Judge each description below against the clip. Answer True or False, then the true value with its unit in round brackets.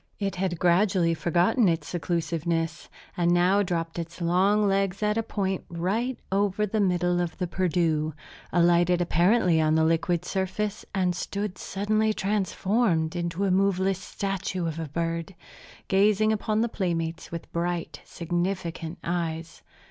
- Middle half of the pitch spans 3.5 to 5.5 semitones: False (2.8 semitones)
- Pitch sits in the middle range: True (180 Hz)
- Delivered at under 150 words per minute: True (140 wpm)